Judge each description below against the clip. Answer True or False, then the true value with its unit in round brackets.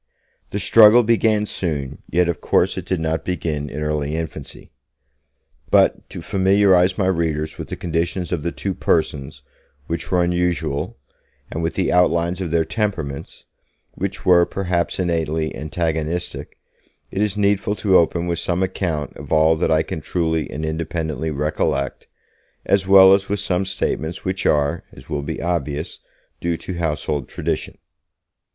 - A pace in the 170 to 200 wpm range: False (155 wpm)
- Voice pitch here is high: False (85 Hz)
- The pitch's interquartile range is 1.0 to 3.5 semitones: True (3.1 semitones)